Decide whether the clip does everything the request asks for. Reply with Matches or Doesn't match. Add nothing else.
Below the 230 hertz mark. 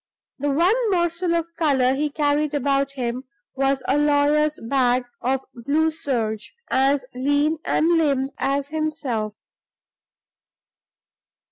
Doesn't match